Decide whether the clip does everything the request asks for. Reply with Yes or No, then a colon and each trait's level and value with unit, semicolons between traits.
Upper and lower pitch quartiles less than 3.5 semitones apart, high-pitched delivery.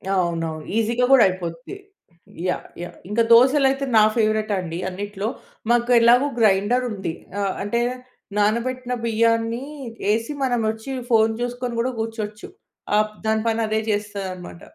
Yes: average, 2.8 semitones; high, 220 Hz